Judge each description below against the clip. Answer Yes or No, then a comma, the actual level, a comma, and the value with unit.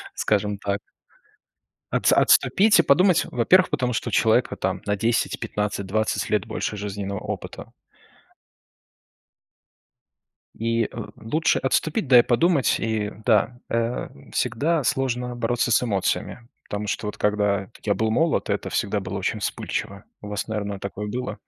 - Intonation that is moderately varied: Yes, average, 3.4 semitones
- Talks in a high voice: No, low, 115 Hz